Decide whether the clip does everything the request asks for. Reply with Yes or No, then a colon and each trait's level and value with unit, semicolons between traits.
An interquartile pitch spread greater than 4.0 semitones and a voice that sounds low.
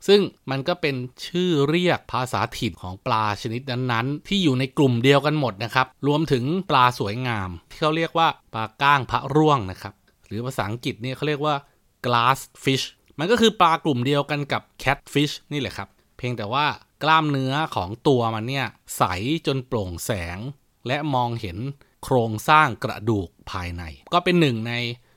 Yes: average, 4.6 semitones; low, 130 Hz